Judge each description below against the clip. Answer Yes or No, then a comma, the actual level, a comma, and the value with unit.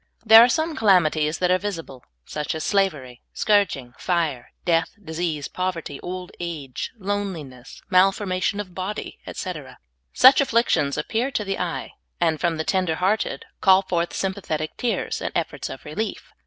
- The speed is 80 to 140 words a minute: No, average, 165 wpm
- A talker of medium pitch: Yes, medium, 180 Hz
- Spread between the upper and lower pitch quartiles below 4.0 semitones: No, average, 4.3 semitones